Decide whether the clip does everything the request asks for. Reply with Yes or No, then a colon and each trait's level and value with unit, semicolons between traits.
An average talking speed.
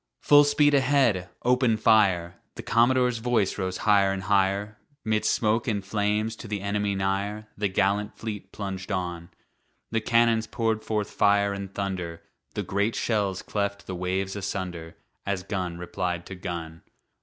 Yes: average, 155 wpm